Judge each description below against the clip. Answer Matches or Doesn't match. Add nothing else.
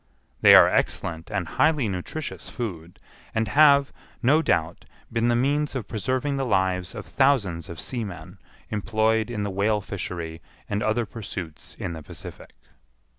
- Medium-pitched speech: Doesn't match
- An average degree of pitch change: Doesn't match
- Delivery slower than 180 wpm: Matches